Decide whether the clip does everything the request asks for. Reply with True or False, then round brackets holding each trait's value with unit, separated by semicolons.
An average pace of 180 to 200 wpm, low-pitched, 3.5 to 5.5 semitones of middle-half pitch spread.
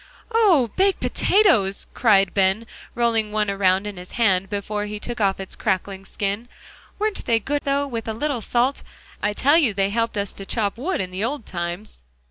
False (190 wpm; 215 Hz; 4.0 semitones)